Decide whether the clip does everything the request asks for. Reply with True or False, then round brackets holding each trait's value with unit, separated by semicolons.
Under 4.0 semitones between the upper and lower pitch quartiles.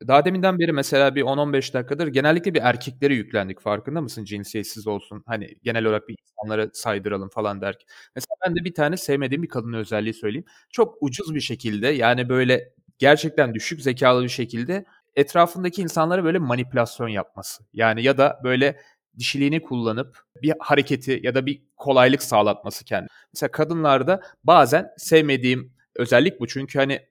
False (5.0 semitones)